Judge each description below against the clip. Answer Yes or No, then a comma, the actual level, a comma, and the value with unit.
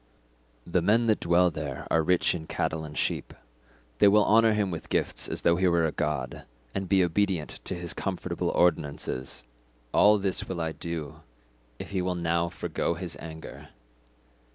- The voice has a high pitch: No, very low, 85 Hz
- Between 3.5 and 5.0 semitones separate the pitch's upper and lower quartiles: No, average, 2.9 semitones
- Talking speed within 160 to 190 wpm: Yes, average, 175 wpm